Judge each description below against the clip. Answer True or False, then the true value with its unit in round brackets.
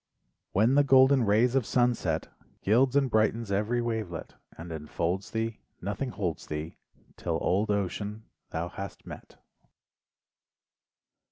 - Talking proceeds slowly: True (120 wpm)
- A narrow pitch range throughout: False (4.7 semitones)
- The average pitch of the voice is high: False (105 Hz)